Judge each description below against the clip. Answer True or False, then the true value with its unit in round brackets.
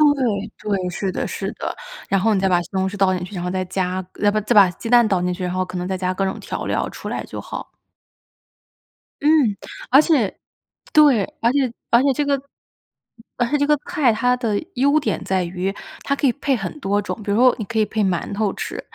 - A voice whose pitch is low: False (205 Hz)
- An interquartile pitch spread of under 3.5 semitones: False (4.9 semitones)